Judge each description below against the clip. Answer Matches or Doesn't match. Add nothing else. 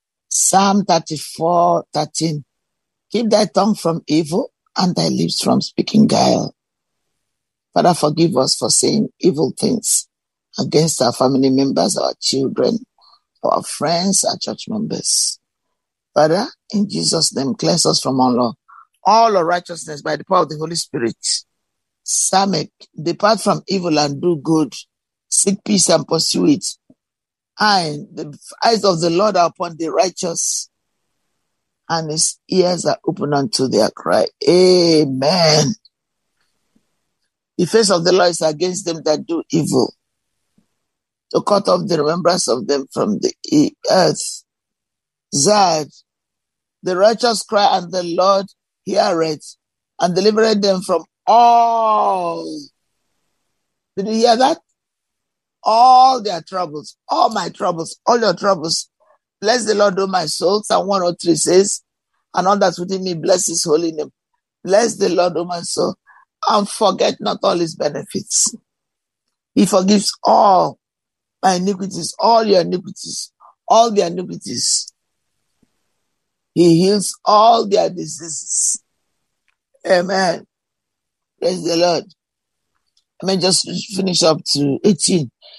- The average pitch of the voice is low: Doesn't match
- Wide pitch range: Doesn't match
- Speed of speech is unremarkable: Doesn't match